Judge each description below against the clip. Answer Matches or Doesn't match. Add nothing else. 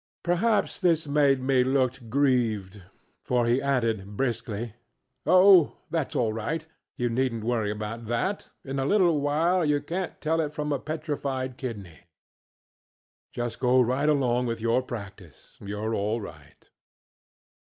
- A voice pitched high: Doesn't match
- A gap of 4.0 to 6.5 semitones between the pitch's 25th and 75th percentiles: Matches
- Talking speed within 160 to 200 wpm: Doesn't match